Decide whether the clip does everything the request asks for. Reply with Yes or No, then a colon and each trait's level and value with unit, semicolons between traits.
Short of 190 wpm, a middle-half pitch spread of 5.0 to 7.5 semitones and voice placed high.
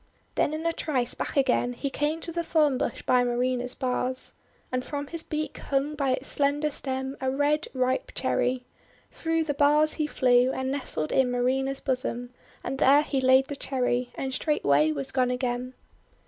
No: average, 180 wpm; average, 2.7 semitones; very high, 265 Hz